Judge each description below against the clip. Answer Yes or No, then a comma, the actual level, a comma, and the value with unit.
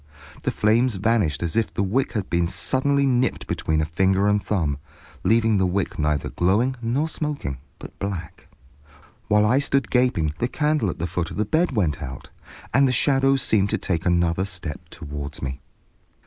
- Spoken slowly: No, average, 180 wpm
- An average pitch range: No, wide, 6.9 semitones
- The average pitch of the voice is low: Yes, low, 100 Hz